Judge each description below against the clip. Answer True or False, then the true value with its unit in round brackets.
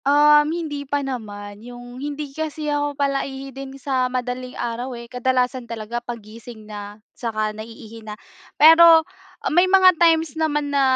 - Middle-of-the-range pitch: False (260 Hz)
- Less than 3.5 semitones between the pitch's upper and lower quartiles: False (4.0 semitones)